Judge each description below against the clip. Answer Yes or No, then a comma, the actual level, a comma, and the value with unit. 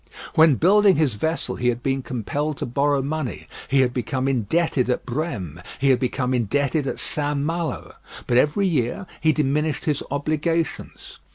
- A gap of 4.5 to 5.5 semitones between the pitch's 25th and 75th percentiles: No, average, 3.8 semitones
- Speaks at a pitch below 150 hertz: Yes, medium, 140 Hz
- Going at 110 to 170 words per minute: Yes, average, 165 wpm